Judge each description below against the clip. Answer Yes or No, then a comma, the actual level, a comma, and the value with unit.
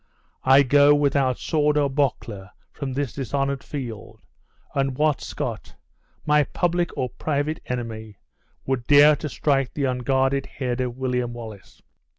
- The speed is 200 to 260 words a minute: No, average, 140 wpm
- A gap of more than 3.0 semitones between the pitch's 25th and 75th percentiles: No, narrow, 2.5 semitones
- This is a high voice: No, low, 135 Hz